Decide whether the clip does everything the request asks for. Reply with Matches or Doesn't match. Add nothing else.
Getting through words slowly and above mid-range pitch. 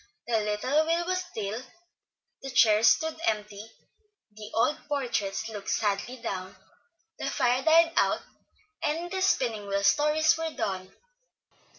Matches